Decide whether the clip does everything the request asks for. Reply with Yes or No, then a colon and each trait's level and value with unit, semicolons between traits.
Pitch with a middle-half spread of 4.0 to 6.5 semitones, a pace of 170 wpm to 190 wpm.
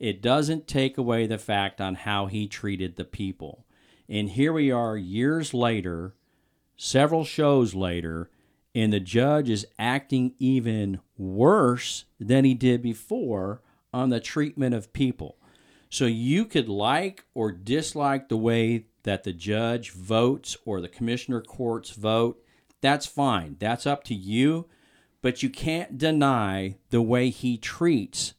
No: average, 4.4 semitones; average, 145 wpm